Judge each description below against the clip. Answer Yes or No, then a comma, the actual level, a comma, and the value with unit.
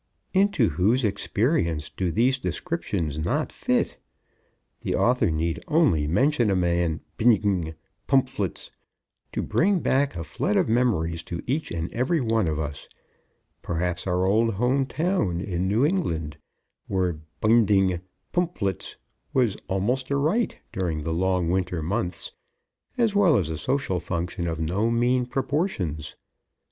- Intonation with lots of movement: Yes, wide, 7.2 semitones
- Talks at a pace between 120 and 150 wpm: Yes, slow, 135 wpm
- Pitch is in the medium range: No, low, 100 Hz